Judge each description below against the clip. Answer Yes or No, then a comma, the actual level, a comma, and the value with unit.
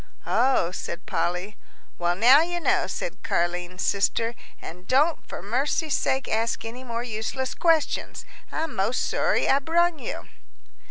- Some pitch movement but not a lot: No, wide, 7.3 semitones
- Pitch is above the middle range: Yes, high, 240 Hz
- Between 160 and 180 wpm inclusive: No, average, 145 wpm